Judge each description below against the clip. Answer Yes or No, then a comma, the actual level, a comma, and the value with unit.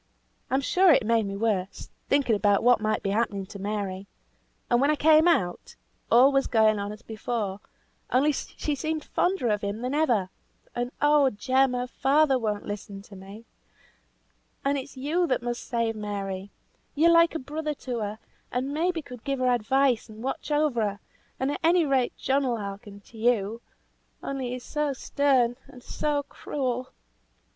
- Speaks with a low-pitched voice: No, high, 245 Hz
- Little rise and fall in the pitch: No, average, 5.0 semitones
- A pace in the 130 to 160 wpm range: No, average, 175 wpm